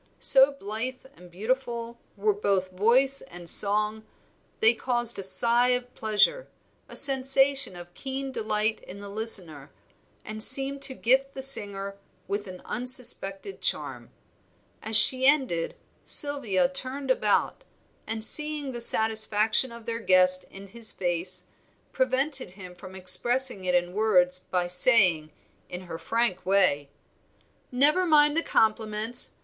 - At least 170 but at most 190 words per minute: No, slow, 135 wpm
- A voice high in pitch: Yes, high, 220 Hz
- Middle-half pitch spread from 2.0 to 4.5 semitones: No, average, 5.3 semitones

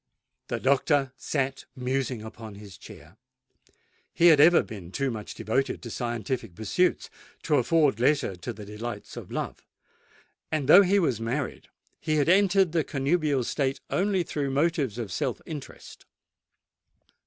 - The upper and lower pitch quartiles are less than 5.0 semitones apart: No, wide, 5.4 semitones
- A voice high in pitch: No, low, 135 Hz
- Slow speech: No, average, 145 wpm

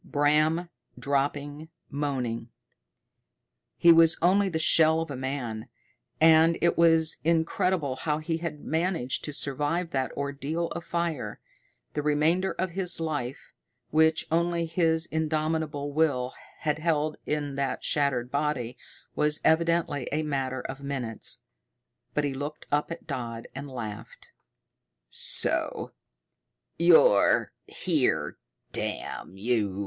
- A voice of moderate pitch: Yes, medium, 150 Hz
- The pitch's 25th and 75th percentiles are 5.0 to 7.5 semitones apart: No, average, 3.0 semitones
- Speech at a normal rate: No, slow, 120 wpm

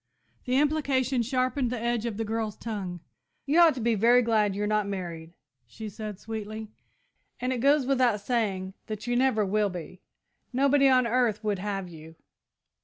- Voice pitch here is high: Yes, high, 225 Hz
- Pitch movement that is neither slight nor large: Yes, average, 3.7 semitones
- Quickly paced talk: No, average, 175 wpm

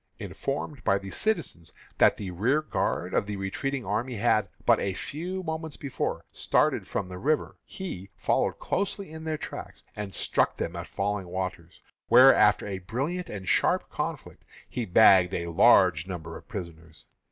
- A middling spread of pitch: No, wide, 7.4 semitones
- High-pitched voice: No, low, 105 Hz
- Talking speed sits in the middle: Yes, average, 160 wpm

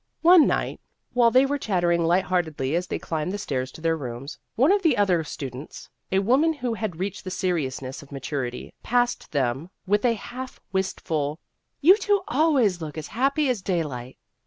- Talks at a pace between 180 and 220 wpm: Yes, average, 185 wpm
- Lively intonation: Yes, wide, 8.5 semitones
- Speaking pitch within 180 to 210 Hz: Yes, medium, 185 Hz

